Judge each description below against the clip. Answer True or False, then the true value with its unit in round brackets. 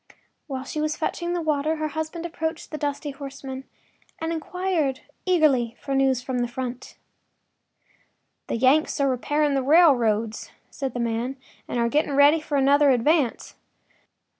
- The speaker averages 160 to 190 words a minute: False (150 wpm)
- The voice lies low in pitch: False (280 Hz)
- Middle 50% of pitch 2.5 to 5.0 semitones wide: True (3.2 semitones)